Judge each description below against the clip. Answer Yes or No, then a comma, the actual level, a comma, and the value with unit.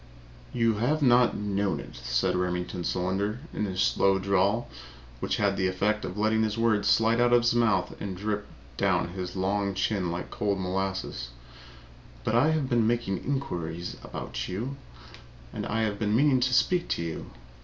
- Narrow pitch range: No, average, 3.9 semitones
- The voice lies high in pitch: No, low, 105 Hz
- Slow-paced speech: No, average, 175 wpm